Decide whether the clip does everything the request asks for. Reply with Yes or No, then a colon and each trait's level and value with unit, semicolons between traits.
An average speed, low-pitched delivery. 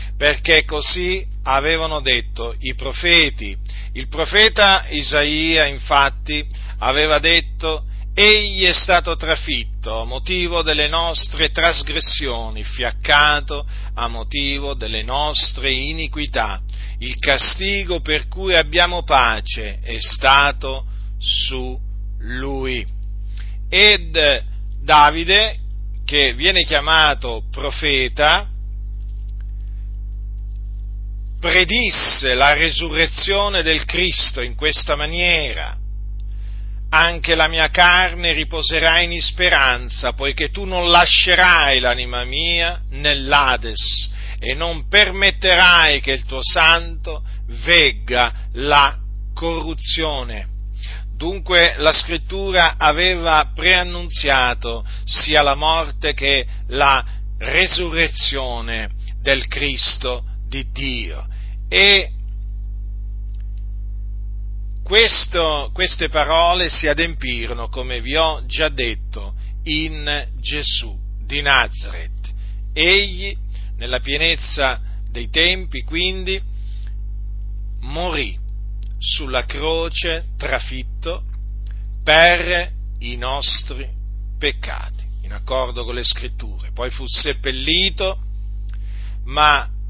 No: slow, 85 wpm; low, 130 Hz